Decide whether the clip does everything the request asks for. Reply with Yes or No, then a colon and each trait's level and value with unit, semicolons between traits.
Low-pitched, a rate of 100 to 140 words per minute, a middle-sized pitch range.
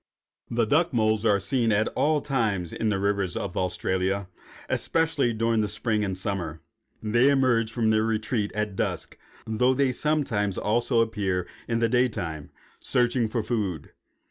No: low, 110 Hz; average, 160 wpm; average, 3.3 semitones